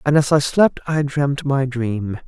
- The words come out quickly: Yes, fast, 210 wpm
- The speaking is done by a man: Yes, male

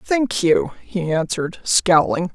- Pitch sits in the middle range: Yes, medium, 180 Hz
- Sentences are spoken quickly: No, slow, 130 wpm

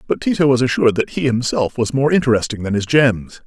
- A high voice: No, low, 125 Hz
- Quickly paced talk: Yes, fast, 225 wpm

